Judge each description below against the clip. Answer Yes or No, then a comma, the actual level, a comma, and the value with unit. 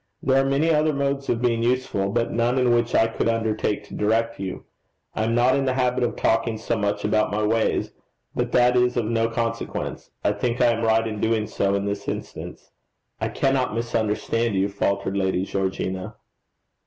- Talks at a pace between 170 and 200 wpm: Yes, average, 195 wpm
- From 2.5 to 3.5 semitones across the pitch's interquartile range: Yes, average, 2.8 semitones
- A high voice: No, low, 115 Hz